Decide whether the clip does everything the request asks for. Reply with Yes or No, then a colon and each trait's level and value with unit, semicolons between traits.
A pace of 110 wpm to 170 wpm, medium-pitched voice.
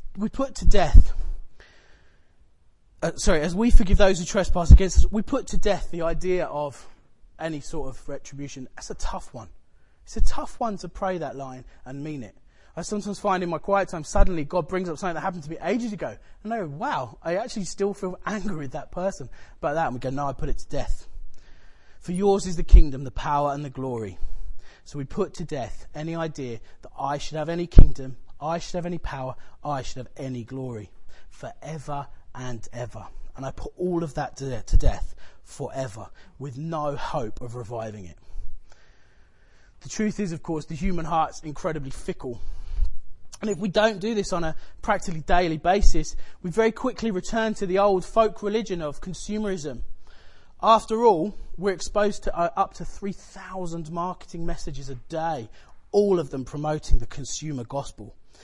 No: average, 190 wpm; medium, 155 Hz